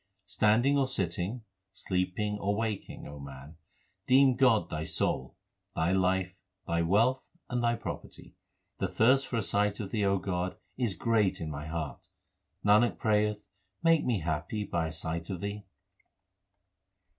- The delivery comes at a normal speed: Yes, average, 150 wpm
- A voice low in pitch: Yes, low, 100 Hz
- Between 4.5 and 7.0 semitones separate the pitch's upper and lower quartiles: Yes, average, 5.0 semitones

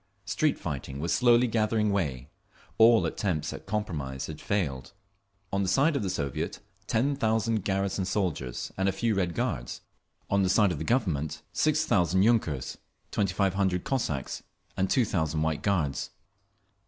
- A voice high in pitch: No, very low, 95 Hz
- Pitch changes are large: Yes, wide, 5.7 semitones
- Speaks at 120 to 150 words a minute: No, average, 160 wpm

